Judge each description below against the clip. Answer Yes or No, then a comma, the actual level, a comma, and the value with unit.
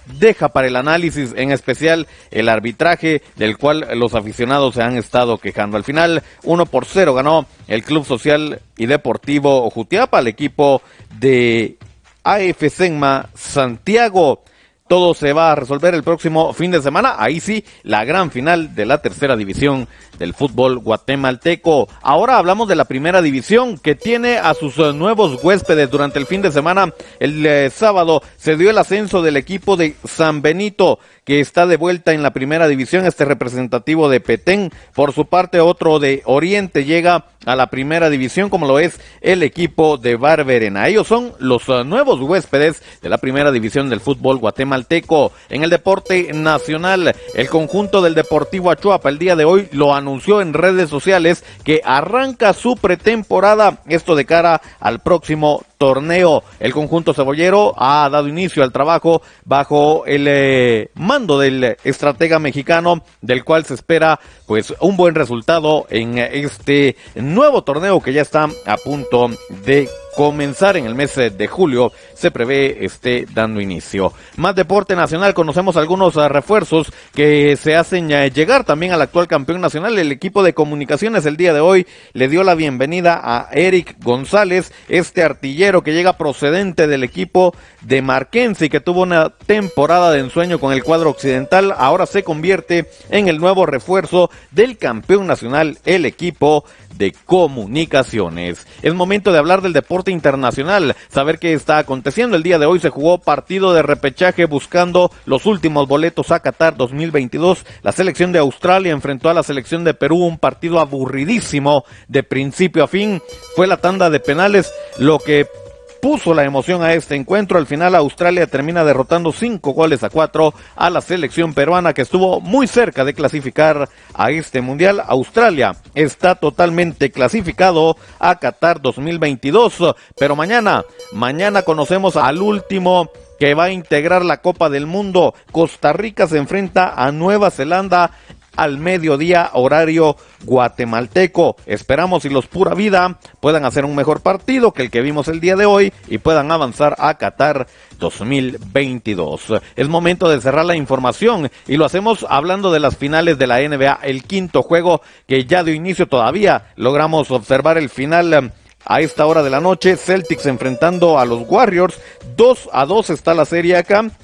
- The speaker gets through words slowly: No, average, 165 wpm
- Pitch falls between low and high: Yes, medium, 155 Hz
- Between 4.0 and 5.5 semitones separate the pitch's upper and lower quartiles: Yes, average, 4.5 semitones